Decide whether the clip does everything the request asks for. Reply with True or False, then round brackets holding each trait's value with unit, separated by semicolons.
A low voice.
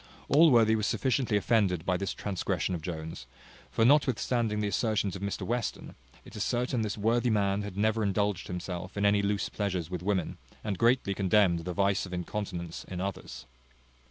True (100 Hz)